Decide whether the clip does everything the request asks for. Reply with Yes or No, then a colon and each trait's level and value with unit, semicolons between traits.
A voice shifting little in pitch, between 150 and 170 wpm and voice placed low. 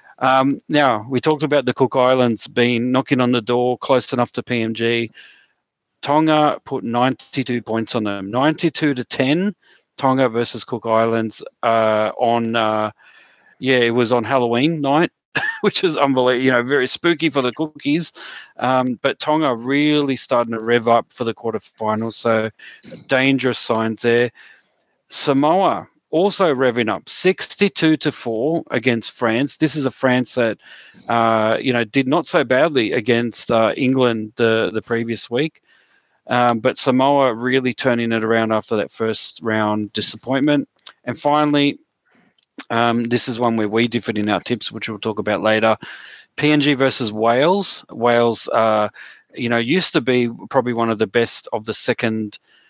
No: average, 3.1 semitones; average, 160 wpm; low, 125 Hz